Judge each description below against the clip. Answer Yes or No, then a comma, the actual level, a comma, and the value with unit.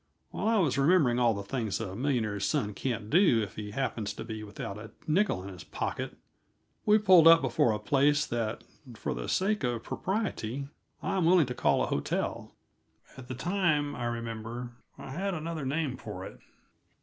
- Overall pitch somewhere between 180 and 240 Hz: No, low, 125 Hz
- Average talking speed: Yes, average, 185 wpm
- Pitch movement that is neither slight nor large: No, wide, 6.8 semitones